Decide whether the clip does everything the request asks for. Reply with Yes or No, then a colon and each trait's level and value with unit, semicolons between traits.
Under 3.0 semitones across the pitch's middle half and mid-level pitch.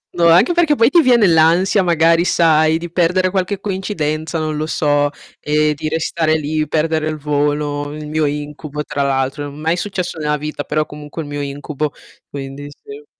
Yes: narrow, 2.6 semitones; medium, 155 Hz